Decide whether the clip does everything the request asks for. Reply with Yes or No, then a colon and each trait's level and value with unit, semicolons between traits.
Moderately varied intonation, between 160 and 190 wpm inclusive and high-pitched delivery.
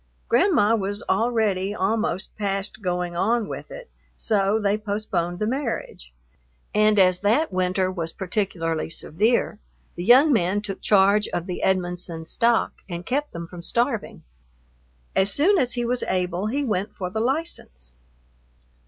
No: average, 4.0 semitones; average, 145 wpm; high, 205 Hz